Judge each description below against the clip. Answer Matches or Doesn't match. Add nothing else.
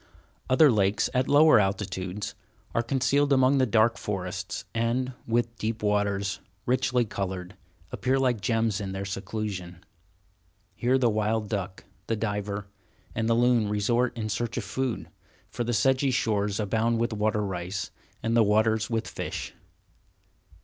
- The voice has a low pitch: Matches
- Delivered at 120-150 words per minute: Matches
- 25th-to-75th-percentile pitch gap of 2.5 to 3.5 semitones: Matches